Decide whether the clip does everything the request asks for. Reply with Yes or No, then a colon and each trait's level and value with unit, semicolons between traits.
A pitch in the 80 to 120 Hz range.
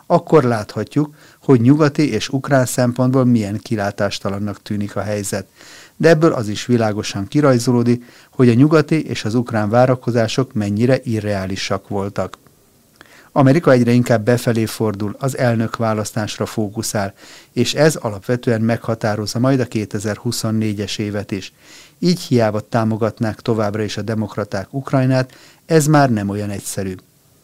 Yes: low, 115 Hz